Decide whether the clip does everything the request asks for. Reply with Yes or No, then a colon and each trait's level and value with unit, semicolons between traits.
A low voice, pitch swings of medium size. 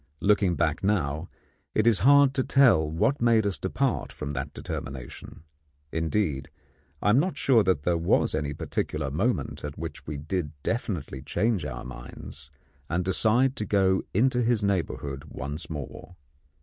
No: very low, 90 Hz; wide, 7.2 semitones